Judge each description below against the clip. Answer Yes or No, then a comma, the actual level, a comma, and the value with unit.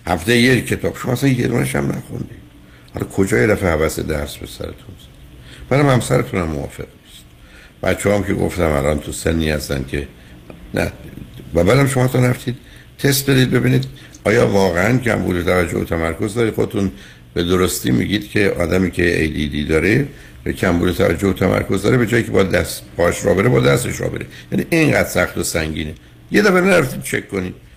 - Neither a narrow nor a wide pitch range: No, wide, 7.8 semitones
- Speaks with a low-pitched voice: Yes, very low, 95 Hz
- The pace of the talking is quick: Yes, fast, 175 wpm